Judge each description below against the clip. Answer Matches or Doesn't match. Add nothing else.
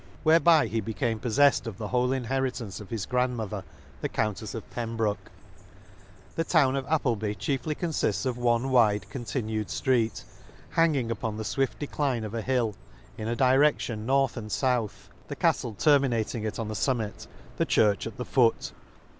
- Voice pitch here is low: Matches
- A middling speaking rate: Matches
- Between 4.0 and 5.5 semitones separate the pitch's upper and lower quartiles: Doesn't match